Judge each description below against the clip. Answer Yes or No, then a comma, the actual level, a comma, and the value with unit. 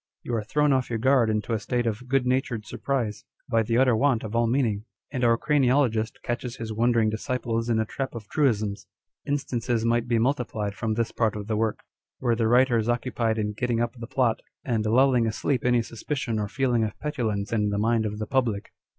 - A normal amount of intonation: No, narrow, 2.3 semitones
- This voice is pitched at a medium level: No, low, 115 Hz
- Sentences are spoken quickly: Yes, fast, 210 wpm